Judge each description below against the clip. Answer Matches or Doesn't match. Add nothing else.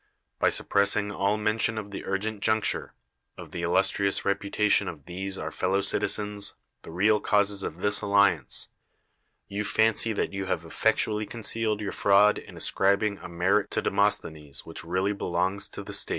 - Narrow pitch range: Matches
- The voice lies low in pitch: Matches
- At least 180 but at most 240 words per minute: Doesn't match